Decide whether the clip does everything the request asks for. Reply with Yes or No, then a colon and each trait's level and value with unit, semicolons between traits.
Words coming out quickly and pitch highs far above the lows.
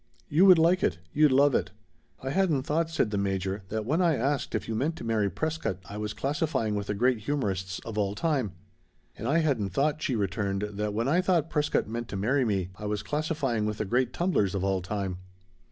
Yes: fast, 220 wpm; wide, 6.6 semitones